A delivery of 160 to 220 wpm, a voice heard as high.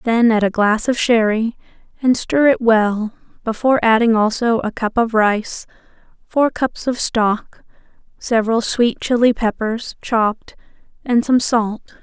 No: average, 145 wpm; high, 230 Hz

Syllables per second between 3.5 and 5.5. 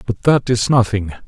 Yes: 5.0 syllables/s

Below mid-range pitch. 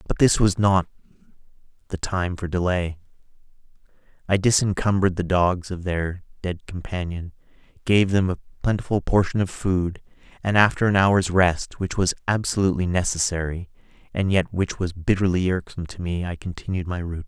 Yes: very low, 90 Hz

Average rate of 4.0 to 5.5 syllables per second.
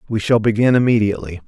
No: 7.1 syllables/s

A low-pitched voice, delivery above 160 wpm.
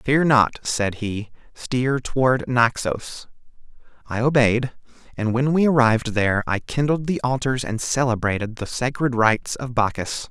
No: low, 120 Hz; average, 145 wpm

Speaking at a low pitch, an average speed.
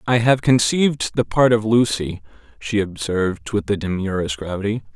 Yes: low, 105 Hz; average, 160 wpm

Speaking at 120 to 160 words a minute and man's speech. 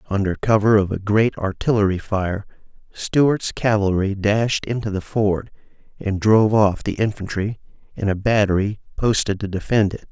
Yes: average, 150 wpm; male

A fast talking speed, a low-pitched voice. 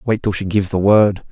Yes: fast, 275 wpm; low, 100 Hz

